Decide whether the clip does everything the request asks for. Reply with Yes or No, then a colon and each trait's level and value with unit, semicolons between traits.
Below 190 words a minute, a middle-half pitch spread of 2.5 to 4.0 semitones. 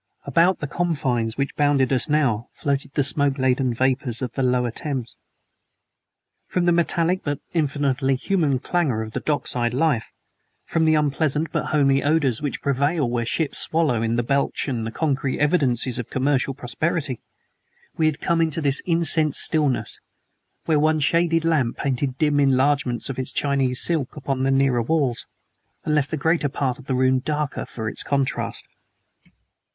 Yes: average, 170 wpm; average, 3.2 semitones